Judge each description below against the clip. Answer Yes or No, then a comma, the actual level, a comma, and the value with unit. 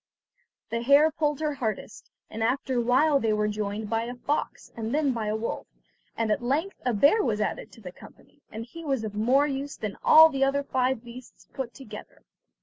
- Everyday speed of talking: No, fast, 210 wpm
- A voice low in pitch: No, very high, 250 Hz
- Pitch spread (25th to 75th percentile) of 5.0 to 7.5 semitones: No, average, 4.2 semitones